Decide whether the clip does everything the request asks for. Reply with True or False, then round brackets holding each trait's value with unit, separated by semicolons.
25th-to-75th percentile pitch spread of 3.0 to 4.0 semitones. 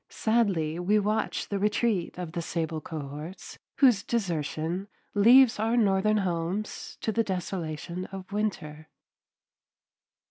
False (4.4 semitones)